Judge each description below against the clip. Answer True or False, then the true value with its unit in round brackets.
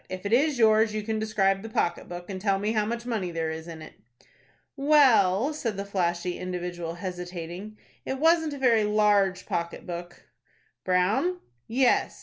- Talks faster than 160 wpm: True (170 wpm)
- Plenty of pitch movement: False (4.3 semitones)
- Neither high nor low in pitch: False (200 Hz)